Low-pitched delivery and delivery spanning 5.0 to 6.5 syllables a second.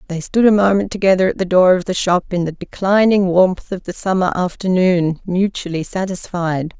No: medium, 185 Hz; 5.1 syllables/s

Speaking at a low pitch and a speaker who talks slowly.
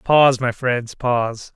Yes: low, 125 Hz; slow, 115 wpm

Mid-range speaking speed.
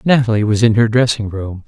No: fast, 215 wpm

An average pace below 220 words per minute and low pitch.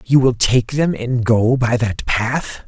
Yes: average, 200 wpm; low, 120 Hz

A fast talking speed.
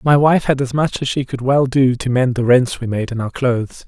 Yes: fast, 295 wpm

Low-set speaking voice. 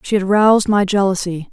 No: high, 195 Hz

